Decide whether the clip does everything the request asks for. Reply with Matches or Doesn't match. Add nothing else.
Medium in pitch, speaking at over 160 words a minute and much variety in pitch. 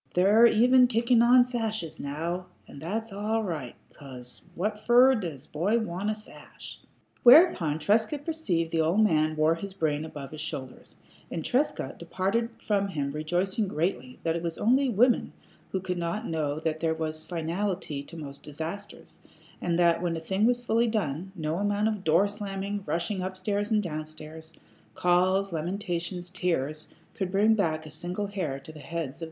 Doesn't match